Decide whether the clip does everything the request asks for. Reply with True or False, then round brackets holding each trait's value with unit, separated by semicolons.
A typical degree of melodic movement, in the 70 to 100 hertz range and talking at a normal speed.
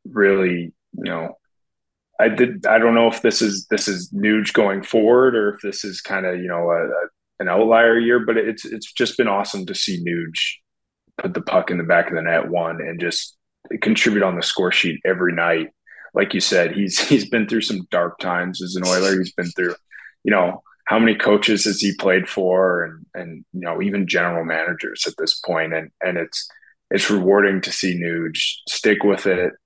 False (3.5 semitones; 95 Hz; 210 wpm)